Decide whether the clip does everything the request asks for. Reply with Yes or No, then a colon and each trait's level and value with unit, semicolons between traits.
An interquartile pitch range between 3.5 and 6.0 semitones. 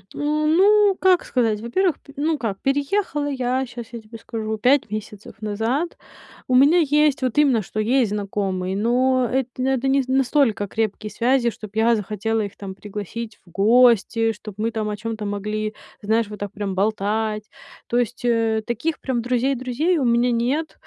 Yes: average, 4.0 semitones